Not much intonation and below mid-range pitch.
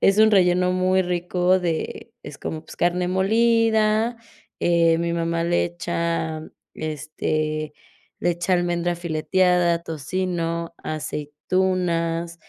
No: narrow, 1.8 semitones; medium, 175 Hz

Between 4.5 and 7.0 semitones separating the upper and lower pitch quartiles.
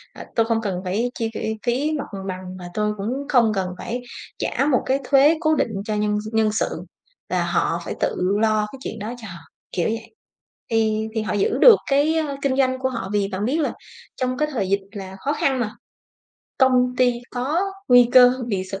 No: average, 3.8 semitones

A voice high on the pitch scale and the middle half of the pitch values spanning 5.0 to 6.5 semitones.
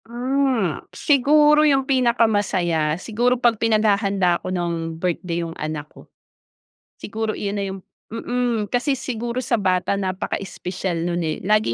Yes: high, 210 Hz; wide, 5.4 semitones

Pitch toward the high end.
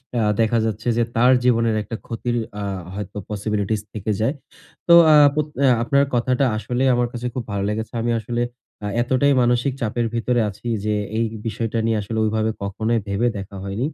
No: low, 115 Hz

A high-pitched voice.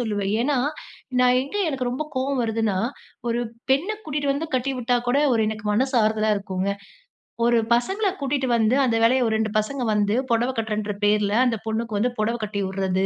Yes: high, 230 Hz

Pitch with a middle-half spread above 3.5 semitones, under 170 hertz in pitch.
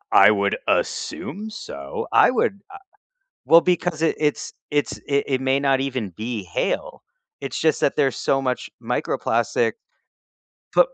Yes: average, 4.1 semitones; low, 135 Hz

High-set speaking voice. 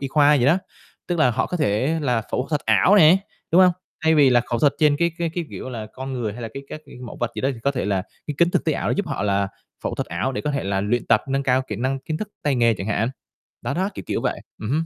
No: low, 135 Hz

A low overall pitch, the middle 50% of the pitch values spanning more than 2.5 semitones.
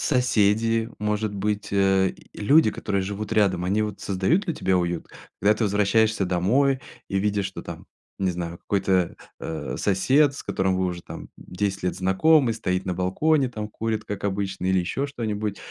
Yes: low, 100 Hz; average, 2.9 semitones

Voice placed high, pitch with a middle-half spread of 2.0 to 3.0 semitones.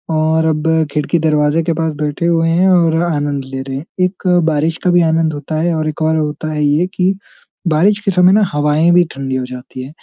No: medium, 160 Hz; narrow, 2.4 semitones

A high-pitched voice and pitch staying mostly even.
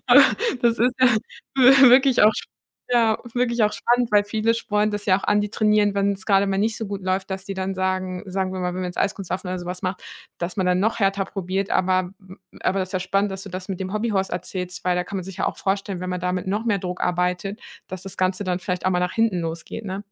Yes: high, 195 Hz; narrow, 2.3 semitones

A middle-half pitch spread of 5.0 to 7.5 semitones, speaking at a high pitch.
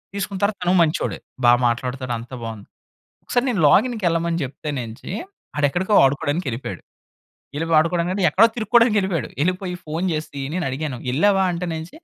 No: wide, 5.5 semitones; medium, 165 Hz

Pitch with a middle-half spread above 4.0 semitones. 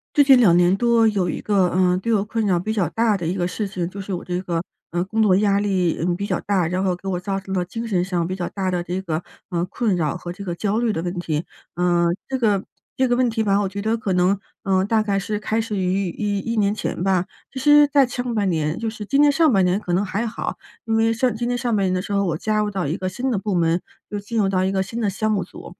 No: average, 3.4 semitones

